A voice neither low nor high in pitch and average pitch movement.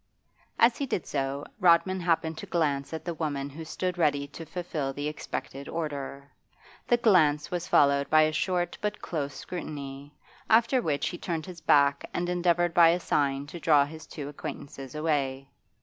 Yes: medium, 155 Hz; average, 3.7 semitones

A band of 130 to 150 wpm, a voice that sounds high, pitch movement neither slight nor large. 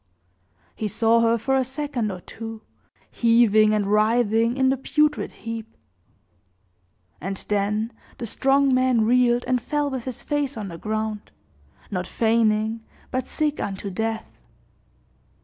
Yes: slow, 135 wpm; high, 230 Hz; average, 3.2 semitones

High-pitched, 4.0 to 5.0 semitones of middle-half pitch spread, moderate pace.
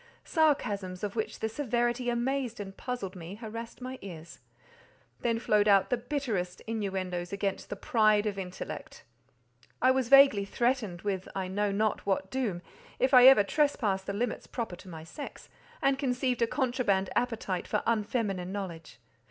Yes: high, 215 Hz; average, 4.3 semitones; average, 160 wpm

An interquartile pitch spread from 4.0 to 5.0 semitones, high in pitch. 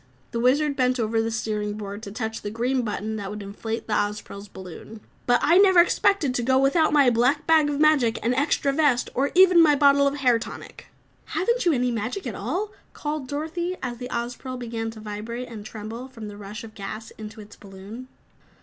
Yes: average, 4.7 semitones; high, 245 Hz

